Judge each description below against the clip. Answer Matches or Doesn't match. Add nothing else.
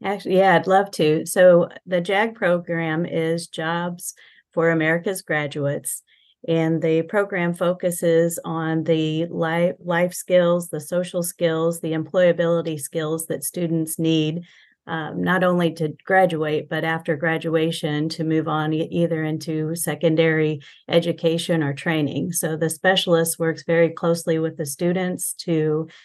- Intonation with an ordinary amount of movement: Doesn't match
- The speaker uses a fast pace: Doesn't match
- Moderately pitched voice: Matches